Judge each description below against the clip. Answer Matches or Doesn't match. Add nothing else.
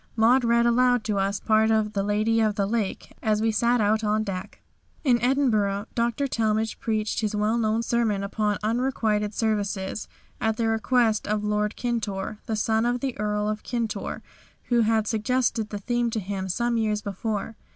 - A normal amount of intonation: Doesn't match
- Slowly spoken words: Doesn't match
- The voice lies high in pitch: Matches